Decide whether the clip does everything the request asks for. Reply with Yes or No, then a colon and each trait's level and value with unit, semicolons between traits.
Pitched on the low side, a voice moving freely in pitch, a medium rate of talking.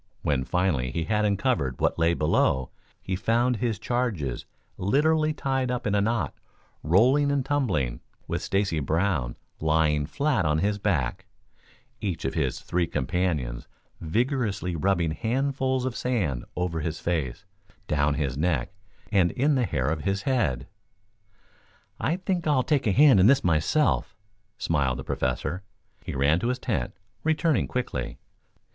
Yes: very low, 95 Hz; wide, 8.7 semitones; average, 150 wpm